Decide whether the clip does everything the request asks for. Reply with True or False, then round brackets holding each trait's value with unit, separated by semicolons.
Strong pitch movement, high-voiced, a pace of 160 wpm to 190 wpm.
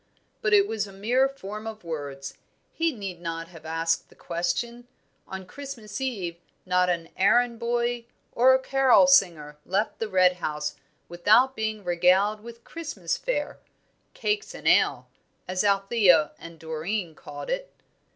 False (5.9 semitones; 200 Hz; 150 wpm)